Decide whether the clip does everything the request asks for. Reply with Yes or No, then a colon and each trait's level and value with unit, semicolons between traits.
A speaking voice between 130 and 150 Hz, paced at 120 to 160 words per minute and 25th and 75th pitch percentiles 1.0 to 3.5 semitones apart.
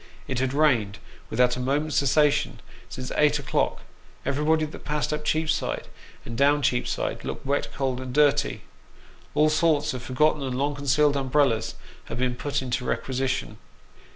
Yes: medium, 140 Hz; average, 155 wpm; average, 2.8 semitones